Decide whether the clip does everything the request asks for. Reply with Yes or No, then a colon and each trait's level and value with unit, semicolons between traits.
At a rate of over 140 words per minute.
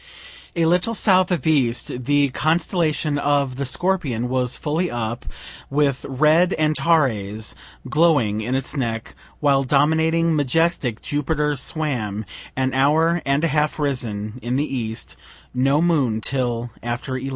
No: slow, 135 wpm